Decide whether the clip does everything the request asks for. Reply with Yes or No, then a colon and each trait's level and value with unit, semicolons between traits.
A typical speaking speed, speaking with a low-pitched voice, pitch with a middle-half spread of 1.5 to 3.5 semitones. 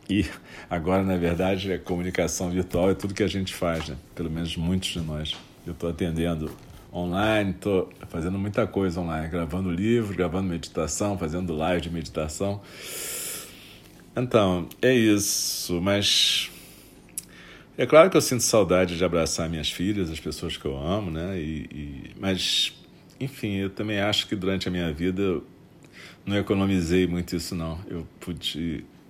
Yes: average, 155 wpm; very low, 90 Hz; narrow, 2.6 semitones